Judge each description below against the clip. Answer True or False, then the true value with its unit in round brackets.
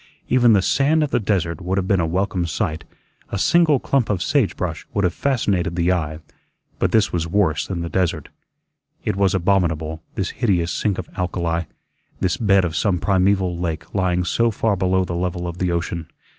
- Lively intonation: False (2.9 semitones)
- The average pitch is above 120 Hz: False (90 Hz)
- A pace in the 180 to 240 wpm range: True (195 wpm)